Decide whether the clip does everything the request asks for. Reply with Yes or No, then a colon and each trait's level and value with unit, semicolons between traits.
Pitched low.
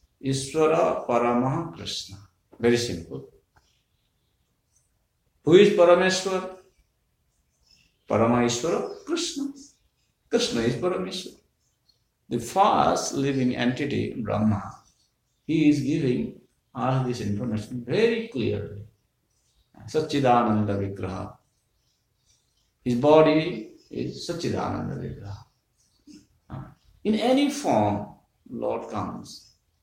Yes: low, 125 Hz